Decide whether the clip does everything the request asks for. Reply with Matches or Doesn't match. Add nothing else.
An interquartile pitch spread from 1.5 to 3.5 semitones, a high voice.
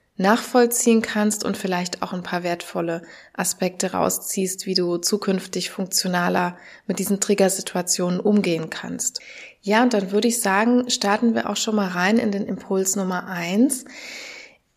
Matches